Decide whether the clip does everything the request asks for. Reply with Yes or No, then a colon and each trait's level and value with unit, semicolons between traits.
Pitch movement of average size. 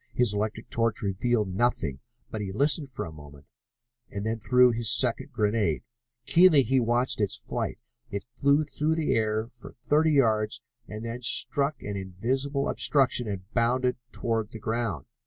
Yes: average, 3.8 semitones